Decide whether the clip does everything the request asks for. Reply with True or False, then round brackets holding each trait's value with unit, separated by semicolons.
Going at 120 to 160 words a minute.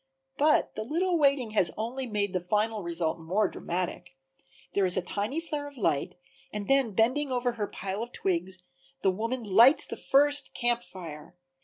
False (175 wpm)